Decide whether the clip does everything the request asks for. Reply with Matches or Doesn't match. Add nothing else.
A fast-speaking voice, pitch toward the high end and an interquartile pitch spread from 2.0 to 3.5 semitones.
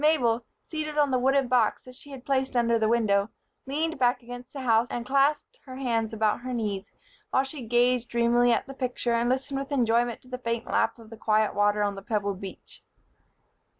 Matches